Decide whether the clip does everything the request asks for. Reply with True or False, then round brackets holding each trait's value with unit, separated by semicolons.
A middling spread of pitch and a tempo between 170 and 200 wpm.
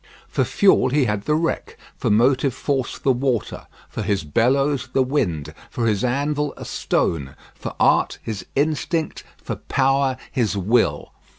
False (4.7 semitones; 155 wpm)